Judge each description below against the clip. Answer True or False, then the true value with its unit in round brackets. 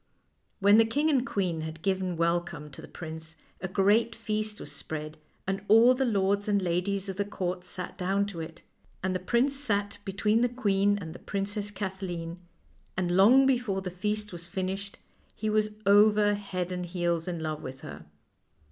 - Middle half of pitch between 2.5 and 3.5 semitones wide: True (3.1 semitones)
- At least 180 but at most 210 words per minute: True (185 wpm)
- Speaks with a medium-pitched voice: False (195 Hz)